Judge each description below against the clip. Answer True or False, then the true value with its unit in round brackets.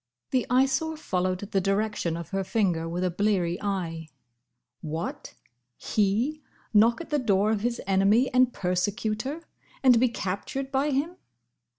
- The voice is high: True (210 Hz)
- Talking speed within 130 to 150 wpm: True (145 wpm)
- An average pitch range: False (5.7 semitones)